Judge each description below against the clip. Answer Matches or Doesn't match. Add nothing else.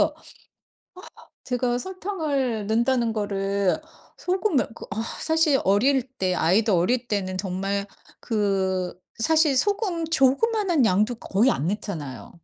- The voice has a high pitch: Matches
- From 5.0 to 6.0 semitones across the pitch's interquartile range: Matches